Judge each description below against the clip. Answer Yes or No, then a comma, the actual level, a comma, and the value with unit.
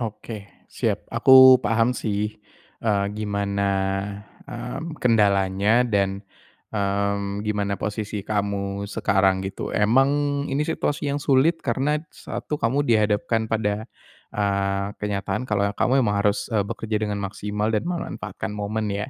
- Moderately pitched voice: No, low, 105 Hz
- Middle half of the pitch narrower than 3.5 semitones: Yes, narrow, 2.6 semitones